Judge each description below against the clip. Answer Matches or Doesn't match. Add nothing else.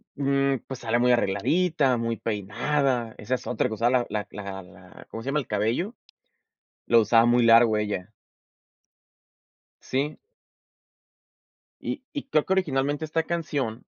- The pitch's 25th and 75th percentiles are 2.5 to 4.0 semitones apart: Doesn't match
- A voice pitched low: Matches